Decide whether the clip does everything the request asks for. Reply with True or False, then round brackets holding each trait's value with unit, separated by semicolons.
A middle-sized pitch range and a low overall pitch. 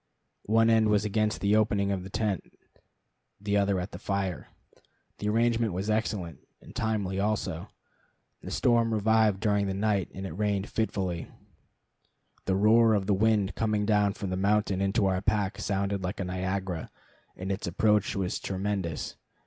False (2.1 semitones; 100 Hz)